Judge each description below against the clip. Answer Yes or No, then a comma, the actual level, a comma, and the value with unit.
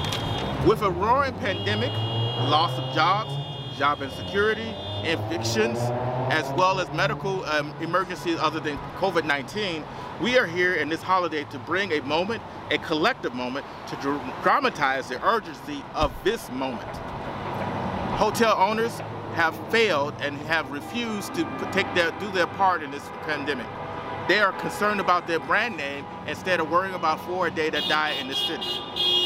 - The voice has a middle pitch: Yes, medium, 155 Hz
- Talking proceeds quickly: No, average, 150 wpm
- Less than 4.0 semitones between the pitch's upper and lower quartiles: No, average, 5.0 semitones